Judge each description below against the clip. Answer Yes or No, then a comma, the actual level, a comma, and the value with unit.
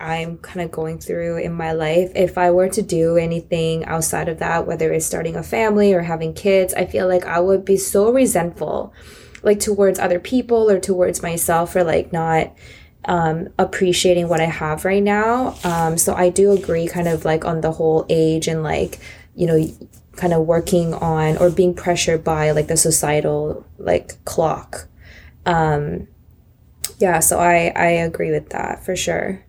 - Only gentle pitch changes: Yes, narrow, 2.2 semitones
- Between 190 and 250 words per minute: No, average, 180 wpm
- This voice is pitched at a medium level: Yes, medium, 170 Hz